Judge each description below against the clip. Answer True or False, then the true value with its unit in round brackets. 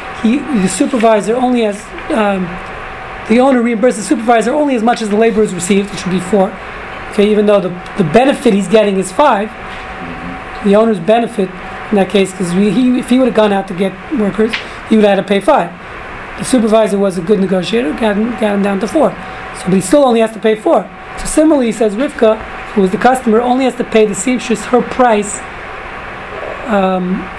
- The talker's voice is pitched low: False (220 Hz)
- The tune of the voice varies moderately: True (3.4 semitones)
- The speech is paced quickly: True (210 wpm)